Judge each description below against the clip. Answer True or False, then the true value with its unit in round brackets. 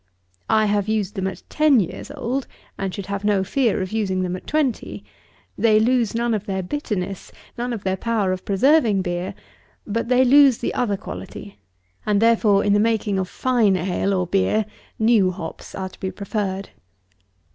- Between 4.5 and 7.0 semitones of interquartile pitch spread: False (3.5 semitones)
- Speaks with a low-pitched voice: False (205 Hz)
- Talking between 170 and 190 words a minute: True (180 wpm)